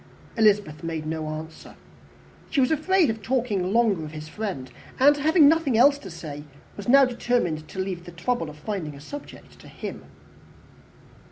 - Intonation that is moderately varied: No, wide, 8.3 semitones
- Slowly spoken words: No, average, 170 wpm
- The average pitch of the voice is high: Yes, high, 205 Hz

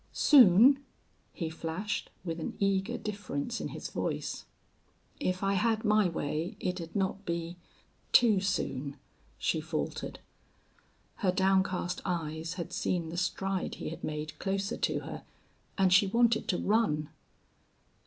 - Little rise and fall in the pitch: No, average, 3.5 semitones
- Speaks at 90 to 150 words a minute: Yes, slow, 135 wpm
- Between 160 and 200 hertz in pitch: Yes, medium, 185 Hz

